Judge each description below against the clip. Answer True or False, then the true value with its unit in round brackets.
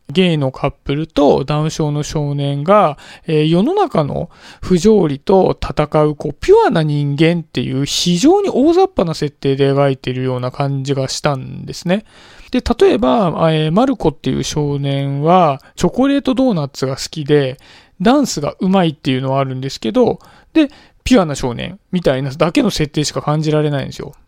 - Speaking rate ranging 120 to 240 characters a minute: False (360 characters per minute)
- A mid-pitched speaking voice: True (155 Hz)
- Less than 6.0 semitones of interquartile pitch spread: True (5.4 semitones)